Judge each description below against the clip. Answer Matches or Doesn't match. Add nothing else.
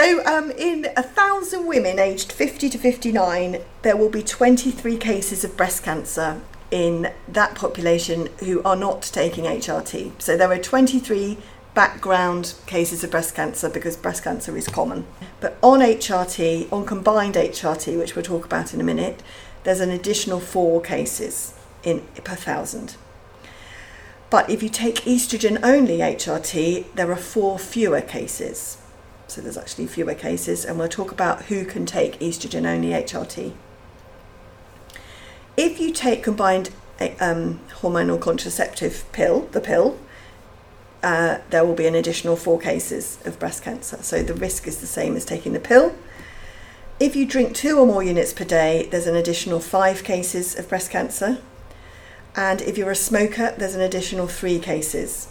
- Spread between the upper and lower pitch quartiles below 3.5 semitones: Doesn't match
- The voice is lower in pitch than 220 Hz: Matches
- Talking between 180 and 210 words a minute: Doesn't match